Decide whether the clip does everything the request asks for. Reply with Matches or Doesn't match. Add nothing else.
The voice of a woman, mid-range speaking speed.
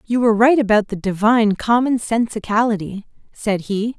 Matches